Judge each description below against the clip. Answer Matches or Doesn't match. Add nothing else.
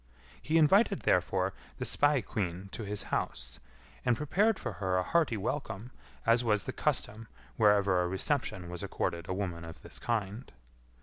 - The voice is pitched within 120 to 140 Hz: Doesn't match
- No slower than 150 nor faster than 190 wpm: Matches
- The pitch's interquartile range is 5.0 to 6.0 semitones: Matches